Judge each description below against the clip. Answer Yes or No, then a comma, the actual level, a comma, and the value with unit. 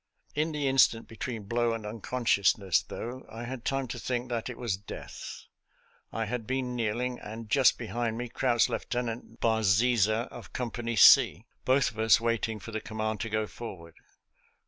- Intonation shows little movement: Yes, narrow, 2.1 semitones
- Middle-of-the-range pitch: No, low, 115 Hz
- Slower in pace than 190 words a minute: Yes, average, 175 wpm